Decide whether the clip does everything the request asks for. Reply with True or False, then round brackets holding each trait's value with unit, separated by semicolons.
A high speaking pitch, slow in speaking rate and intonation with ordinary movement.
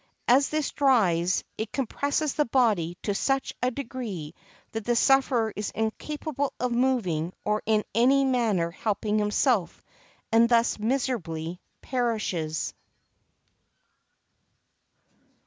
True (230 Hz; 110 wpm; 4.7 semitones)